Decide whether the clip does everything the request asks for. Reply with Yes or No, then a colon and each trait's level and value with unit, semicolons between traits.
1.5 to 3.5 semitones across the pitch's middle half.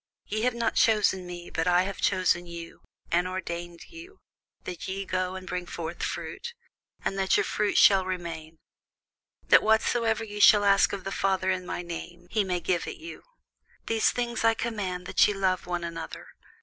Yes: average, 3.2 semitones